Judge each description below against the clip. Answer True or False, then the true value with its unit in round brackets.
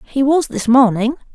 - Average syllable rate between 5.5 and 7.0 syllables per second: False (4.9 syllables/s)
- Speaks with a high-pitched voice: True (255 Hz)